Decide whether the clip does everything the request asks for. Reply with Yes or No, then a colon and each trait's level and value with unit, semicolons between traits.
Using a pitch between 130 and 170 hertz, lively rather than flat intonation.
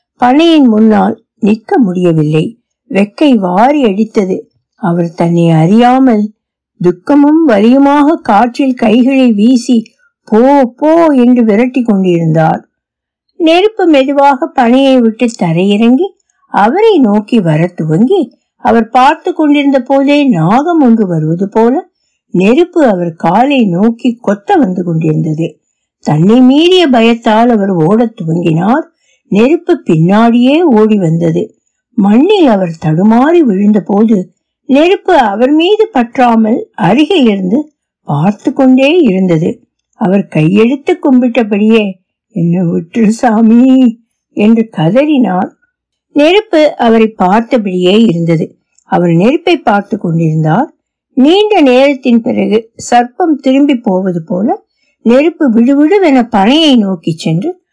No: high, 235 Hz; wide, 6.2 semitones